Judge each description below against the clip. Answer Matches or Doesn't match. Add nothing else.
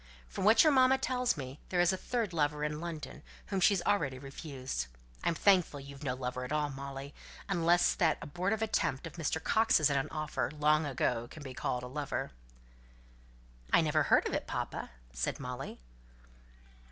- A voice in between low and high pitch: Matches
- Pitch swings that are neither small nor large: Matches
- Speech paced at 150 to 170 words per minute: Doesn't match